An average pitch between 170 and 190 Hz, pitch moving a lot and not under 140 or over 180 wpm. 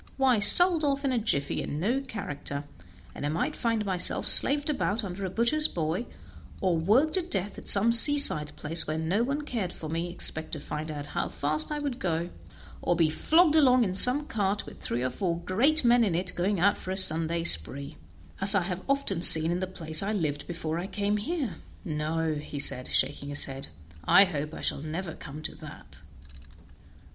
No: medium, 185 Hz; wide, 7.0 semitones; fast, 205 wpm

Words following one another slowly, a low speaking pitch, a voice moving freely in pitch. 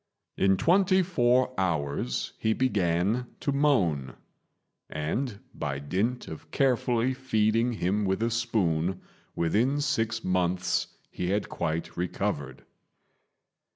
Yes: slow, 110 wpm; low, 105 Hz; wide, 6.3 semitones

